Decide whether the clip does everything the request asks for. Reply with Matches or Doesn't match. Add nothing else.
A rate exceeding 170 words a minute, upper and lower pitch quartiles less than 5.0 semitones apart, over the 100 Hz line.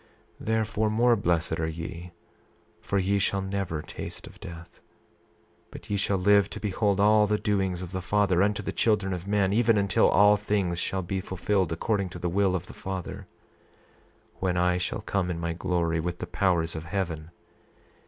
Doesn't match